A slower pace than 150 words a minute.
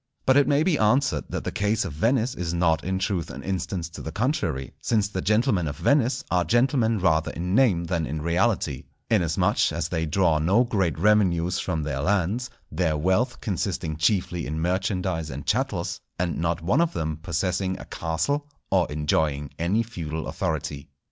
No: average, 175 wpm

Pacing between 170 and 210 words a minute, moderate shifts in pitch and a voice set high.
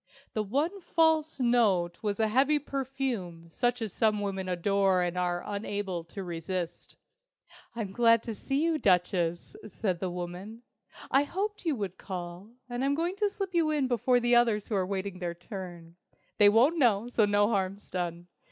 No: average, 175 wpm; wide, 6.0 semitones; high, 205 Hz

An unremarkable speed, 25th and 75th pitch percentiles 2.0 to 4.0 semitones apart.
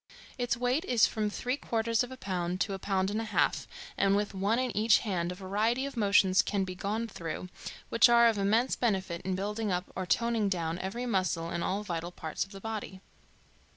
No: fast, 215 wpm; average, 3.6 semitones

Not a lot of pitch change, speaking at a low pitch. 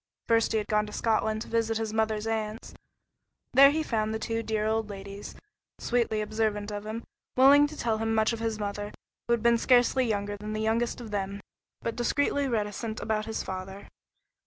No: narrow, 1.5 semitones; high, 220 Hz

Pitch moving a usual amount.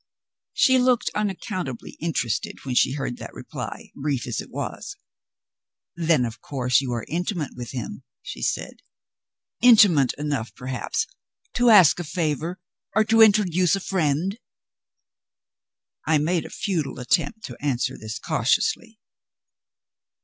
No: wide, 7.2 semitones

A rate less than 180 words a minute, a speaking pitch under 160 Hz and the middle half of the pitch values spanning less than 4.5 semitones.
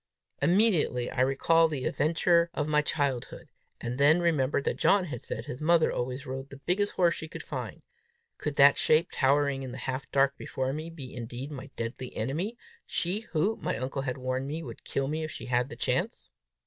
No: average, 200 wpm; medium, 140 Hz; average, 4.0 semitones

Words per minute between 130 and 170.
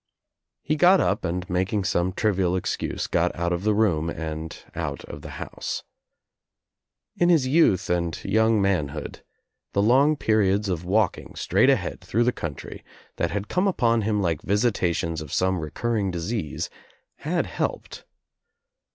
Yes: average, 150 wpm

